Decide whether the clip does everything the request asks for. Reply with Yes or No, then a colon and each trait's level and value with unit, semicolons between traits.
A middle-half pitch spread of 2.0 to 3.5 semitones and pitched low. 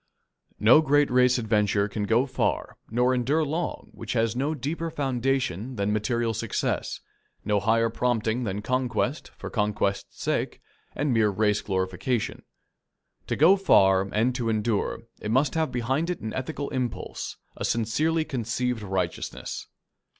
No: average, 4.1 semitones; low, 120 Hz